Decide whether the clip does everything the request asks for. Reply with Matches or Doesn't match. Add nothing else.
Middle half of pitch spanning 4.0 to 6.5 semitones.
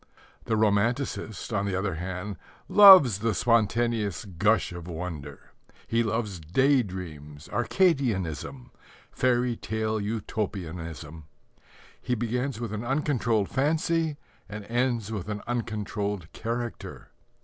Matches